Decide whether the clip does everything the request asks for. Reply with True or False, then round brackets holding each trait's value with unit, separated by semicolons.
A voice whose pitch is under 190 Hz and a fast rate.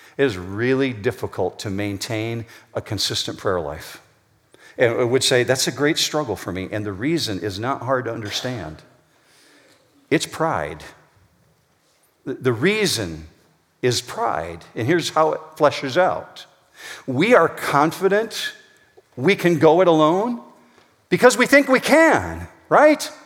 False (140 Hz; 140 wpm)